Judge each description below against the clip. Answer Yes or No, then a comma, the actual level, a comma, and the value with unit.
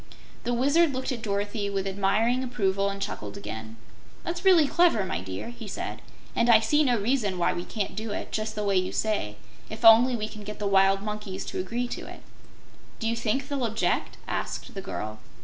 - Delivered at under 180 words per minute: No, fast, 205 wpm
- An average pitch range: Yes, average, 3.7 semitones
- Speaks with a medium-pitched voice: No, high, 215 Hz